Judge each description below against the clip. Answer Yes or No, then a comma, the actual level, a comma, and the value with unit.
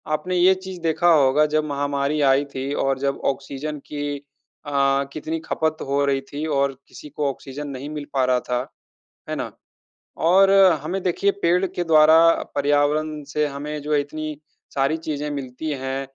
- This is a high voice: No, medium, 145 Hz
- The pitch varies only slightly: Yes, narrow, 2.0 semitones